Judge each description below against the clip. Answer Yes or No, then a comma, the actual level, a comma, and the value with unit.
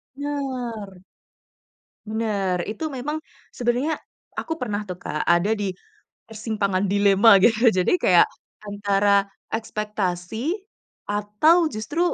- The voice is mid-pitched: No, high, 215 Hz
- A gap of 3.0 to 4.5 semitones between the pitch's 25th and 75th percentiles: Yes, average, 3.6 semitones